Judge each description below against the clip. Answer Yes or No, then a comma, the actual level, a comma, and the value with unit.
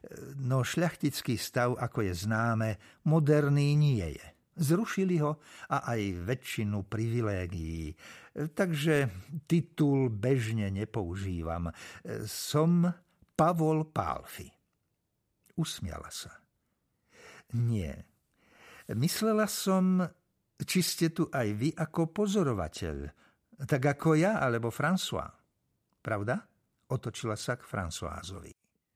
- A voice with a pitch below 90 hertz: No, low, 135 Hz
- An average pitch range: No, wide, 7.0 semitones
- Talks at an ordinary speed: No, slow, 90 wpm